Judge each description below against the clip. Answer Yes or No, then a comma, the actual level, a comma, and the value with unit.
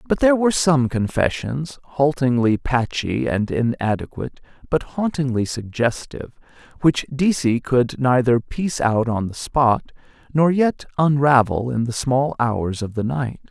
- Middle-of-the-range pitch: No, low, 130 Hz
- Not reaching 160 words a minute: Yes, average, 140 wpm